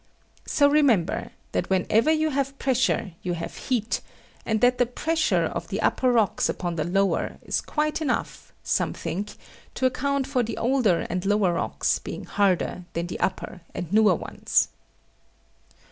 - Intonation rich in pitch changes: Yes, wide, 6.6 semitones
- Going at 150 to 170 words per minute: Yes, average, 160 wpm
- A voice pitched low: No, high, 225 Hz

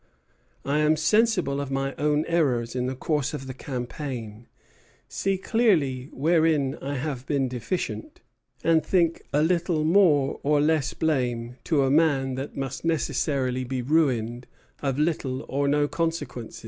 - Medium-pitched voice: Yes, medium, 145 Hz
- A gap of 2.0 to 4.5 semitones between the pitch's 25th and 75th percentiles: Yes, average, 3.6 semitones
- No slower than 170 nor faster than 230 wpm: No, average, 150 wpm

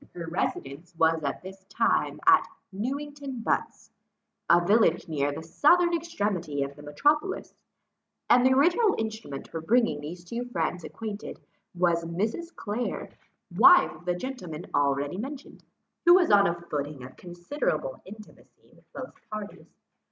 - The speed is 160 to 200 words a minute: No, average, 145 wpm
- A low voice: No, high, 195 Hz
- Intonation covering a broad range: Yes, wide, 8.2 semitones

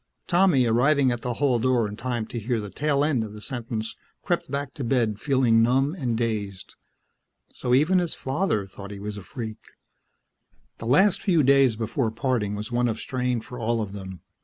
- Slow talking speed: No, average, 195 wpm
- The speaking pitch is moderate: No, low, 120 Hz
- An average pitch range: Yes, average, 3.7 semitones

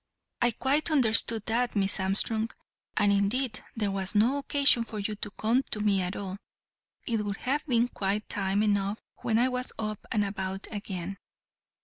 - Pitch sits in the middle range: No, high, 215 Hz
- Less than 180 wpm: Yes, average, 170 wpm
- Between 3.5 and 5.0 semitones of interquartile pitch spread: No, average, 3.1 semitones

